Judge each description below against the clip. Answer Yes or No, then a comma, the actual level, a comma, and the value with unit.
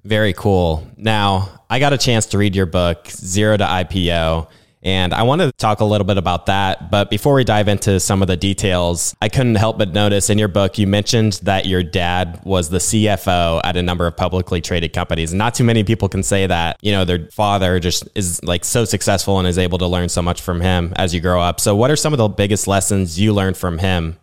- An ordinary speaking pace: No, fast, 240 wpm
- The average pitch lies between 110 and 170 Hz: No, very low, 95 Hz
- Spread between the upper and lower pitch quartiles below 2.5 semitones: No, average, 2.8 semitones